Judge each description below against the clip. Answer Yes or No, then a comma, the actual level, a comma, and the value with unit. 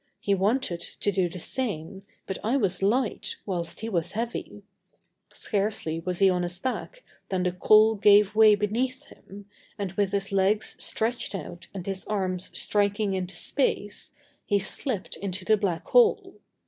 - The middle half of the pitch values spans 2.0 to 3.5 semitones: Yes, average, 2.7 semitones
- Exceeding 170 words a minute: No, average, 160 wpm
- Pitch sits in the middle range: No, high, 200 Hz